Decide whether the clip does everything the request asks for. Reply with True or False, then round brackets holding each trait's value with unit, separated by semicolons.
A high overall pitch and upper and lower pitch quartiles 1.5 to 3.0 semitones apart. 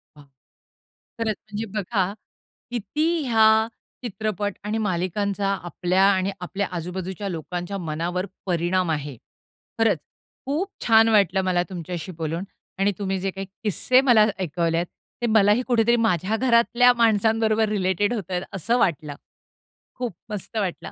False (195 Hz; 3.8 semitones)